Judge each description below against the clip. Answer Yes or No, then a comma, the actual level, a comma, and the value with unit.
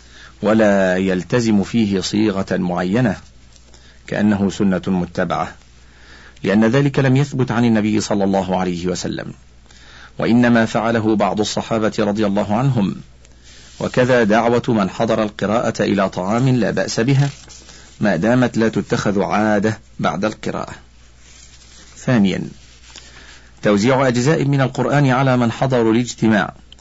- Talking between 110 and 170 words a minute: Yes, average, 115 wpm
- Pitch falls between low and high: No, low, 105 Hz